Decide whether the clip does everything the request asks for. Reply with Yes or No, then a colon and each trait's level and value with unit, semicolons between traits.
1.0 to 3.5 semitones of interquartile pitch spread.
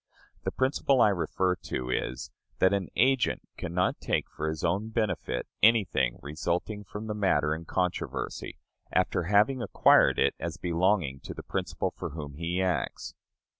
No: average, 4.8 semitones